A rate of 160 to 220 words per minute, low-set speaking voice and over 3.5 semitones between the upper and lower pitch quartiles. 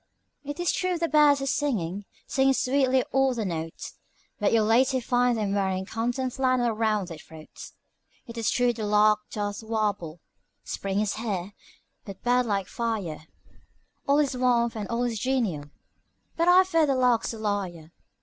No: average, 170 wpm; high, 230 Hz; average, 4.3 semitones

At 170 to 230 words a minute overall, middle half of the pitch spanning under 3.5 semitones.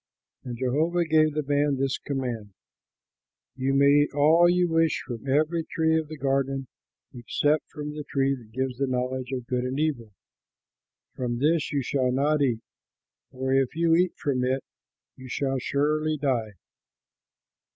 No: average, 160 wpm; average, 3.0 semitones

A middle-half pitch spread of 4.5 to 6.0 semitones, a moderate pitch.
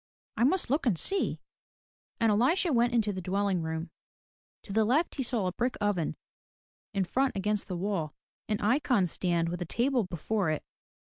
No: average, 5.2 semitones; high, 210 Hz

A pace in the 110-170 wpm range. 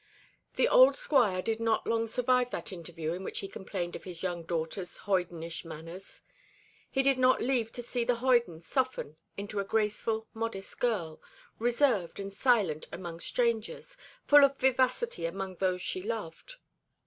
Yes: average, 160 wpm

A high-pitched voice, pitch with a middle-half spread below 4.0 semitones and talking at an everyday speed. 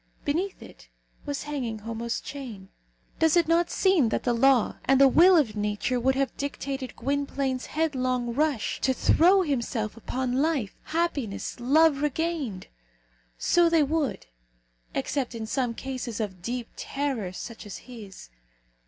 No: very high, 265 Hz; average, 4.4 semitones; average, 145 wpm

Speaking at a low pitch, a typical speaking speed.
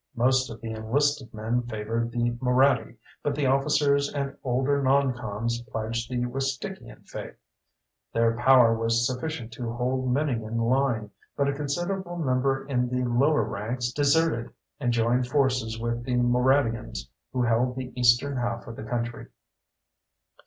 Yes: low, 125 Hz; average, 150 wpm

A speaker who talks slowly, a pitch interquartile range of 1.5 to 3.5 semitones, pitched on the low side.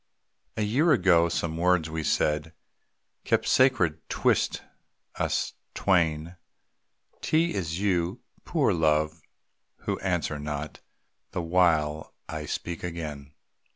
Yes: slow, 110 wpm; average, 2.8 semitones; very low, 85 Hz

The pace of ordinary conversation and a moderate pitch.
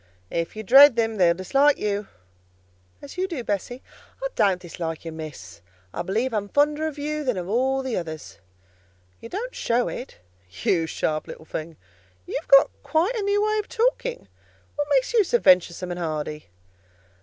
No: average, 180 wpm; high, 235 Hz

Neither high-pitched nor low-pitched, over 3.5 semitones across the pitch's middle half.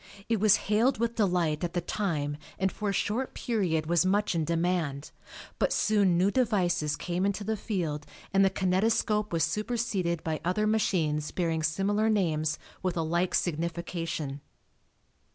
Yes: medium, 180 Hz; average, 4.3 semitones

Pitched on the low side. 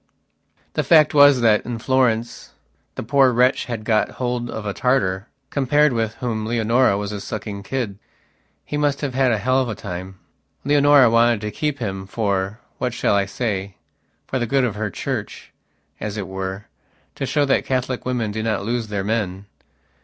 Yes: low, 115 Hz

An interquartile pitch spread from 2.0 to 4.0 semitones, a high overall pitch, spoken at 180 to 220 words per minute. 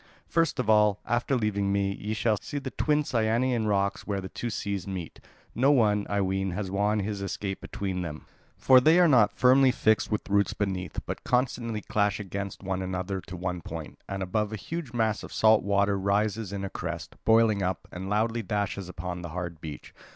No: average, 2.8 semitones; low, 100 Hz; average, 200 wpm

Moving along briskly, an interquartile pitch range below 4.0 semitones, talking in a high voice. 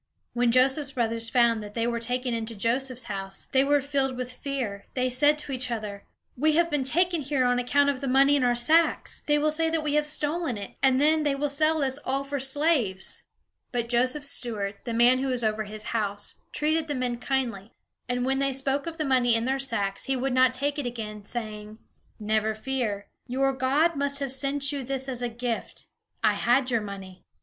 Yes: fast, 215 wpm; average, 3.4 semitones; very high, 255 Hz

